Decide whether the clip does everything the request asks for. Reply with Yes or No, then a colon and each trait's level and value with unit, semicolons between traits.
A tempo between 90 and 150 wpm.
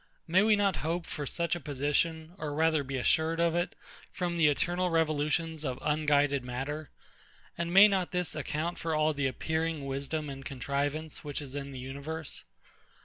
No: average, 175 wpm